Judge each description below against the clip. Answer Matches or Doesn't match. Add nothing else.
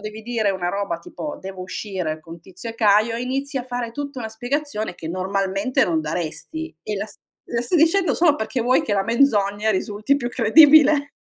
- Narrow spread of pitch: Doesn't match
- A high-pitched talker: Matches